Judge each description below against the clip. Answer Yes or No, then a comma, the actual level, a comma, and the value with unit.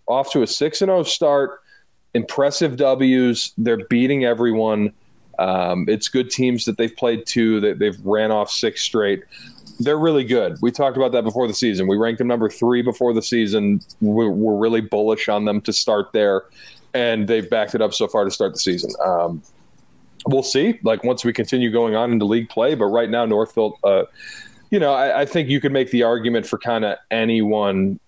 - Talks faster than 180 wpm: Yes, average, 200 wpm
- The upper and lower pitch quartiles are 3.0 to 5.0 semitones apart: Yes, average, 3.3 semitones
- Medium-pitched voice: No, low, 115 Hz